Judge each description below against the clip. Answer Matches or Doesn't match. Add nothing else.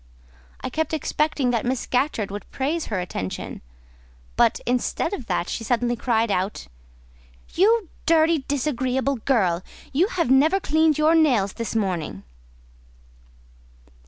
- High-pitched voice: Matches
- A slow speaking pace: Matches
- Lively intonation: Matches